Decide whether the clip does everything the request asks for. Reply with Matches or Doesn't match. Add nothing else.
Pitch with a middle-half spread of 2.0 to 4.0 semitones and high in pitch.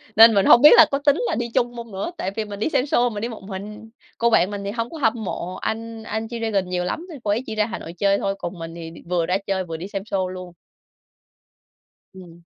Matches